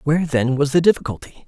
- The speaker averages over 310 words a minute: No, fast, 205 wpm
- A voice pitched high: No, medium, 145 Hz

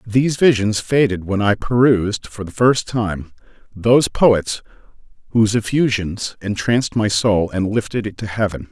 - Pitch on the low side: Yes, low, 105 Hz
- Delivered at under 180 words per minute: Yes, average, 150 wpm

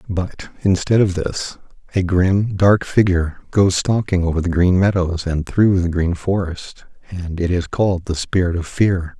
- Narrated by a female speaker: No, male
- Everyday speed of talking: Yes, average, 175 wpm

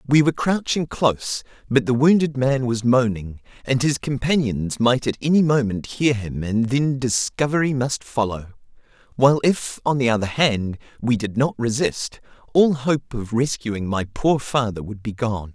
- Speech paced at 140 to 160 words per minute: No, average, 170 wpm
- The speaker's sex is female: No, male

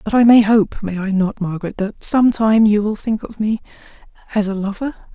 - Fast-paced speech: Yes, fast, 220 wpm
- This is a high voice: Yes, high, 210 Hz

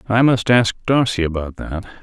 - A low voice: Yes, low, 105 Hz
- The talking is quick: No, average, 180 wpm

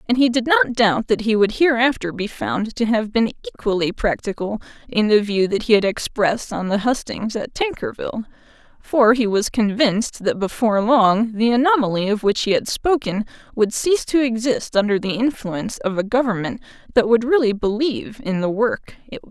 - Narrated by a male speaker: No, female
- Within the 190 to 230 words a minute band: Yes, average, 195 wpm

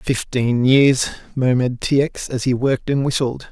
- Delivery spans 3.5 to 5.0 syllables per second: Yes, 4.7 syllables/s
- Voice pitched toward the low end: Yes, low, 130 Hz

